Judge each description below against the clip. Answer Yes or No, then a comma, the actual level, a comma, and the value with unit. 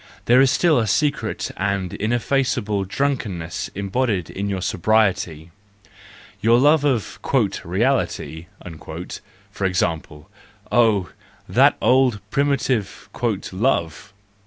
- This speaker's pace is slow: Yes, slow, 110 wpm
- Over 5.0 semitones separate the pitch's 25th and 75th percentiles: Yes, wide, 5.5 semitones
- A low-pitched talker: Yes, low, 105 Hz